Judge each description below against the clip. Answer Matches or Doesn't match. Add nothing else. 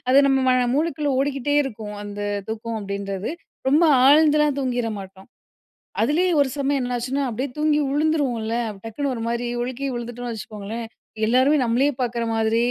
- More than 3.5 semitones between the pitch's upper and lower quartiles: Matches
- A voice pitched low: Doesn't match